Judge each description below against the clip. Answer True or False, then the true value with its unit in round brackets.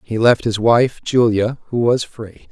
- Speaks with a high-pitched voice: False (115 Hz)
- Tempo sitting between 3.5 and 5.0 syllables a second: True (4.0 syllables/s)